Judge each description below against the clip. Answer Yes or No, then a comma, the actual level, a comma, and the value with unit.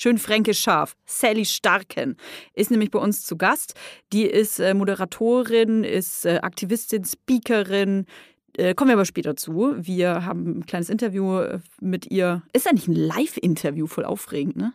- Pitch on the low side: No, high, 205 Hz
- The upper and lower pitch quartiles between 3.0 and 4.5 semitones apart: Yes, average, 3.7 semitones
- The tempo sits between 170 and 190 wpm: No, average, 150 wpm